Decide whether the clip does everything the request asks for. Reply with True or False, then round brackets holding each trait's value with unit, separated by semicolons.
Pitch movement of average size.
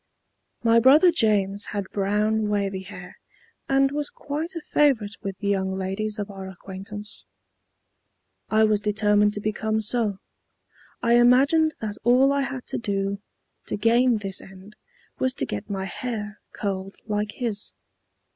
True (3.4 semitones)